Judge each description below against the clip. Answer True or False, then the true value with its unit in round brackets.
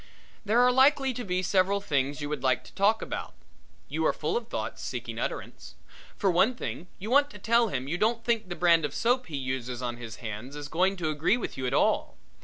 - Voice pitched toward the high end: False (180 Hz)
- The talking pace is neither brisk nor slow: False (230 wpm)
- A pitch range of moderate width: False (8.5 semitones)